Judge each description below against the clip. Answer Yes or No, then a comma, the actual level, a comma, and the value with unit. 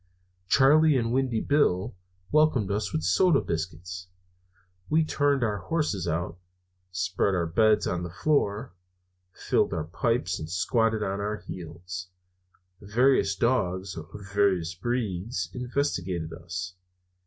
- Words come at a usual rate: No, slow, 120 wpm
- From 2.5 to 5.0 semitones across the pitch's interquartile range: No, wide, 5.5 semitones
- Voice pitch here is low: Yes, low, 100 Hz